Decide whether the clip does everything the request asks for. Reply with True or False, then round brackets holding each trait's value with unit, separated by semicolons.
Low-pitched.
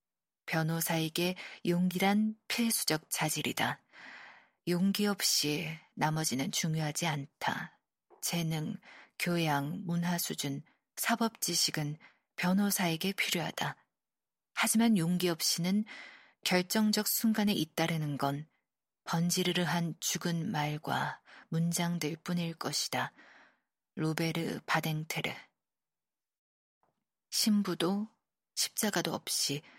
False (170 Hz)